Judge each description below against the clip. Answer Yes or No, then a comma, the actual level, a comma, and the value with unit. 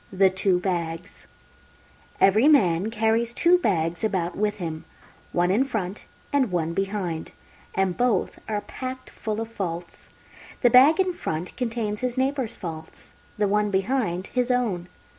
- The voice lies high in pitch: Yes, high, 205 Hz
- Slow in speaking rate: No, average, 145 wpm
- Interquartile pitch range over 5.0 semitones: Yes, wide, 5.4 semitones